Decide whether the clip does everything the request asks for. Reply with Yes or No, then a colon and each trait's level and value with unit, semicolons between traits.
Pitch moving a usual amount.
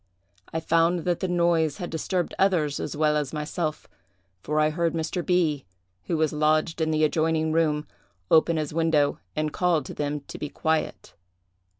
No: narrow, 1.7 semitones